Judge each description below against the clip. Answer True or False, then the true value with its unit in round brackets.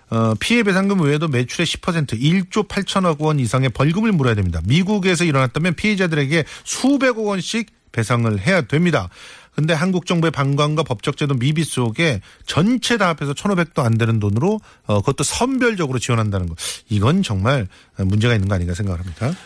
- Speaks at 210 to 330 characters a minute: False (375 characters per minute)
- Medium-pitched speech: True (150 Hz)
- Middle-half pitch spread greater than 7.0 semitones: True (8.0 semitones)